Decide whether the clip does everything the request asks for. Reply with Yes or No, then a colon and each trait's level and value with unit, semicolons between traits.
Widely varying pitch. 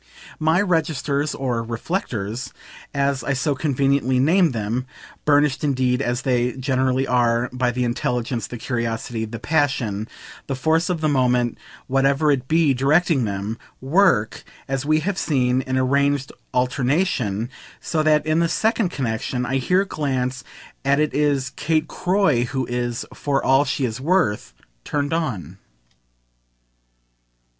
No: average, 3.6 semitones